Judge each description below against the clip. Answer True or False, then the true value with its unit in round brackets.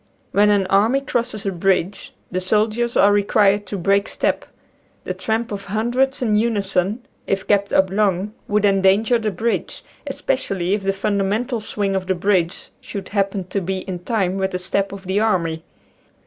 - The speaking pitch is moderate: False (200 Hz)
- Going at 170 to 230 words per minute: True (175 wpm)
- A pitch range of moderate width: False (2.2 semitones)